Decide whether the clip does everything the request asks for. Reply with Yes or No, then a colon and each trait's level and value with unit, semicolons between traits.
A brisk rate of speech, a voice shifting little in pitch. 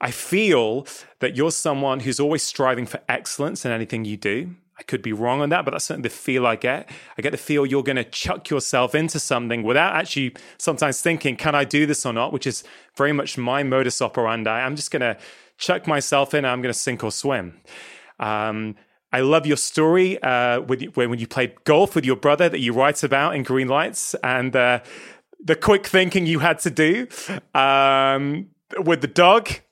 No: fast, 210 wpm; average, 4.0 semitones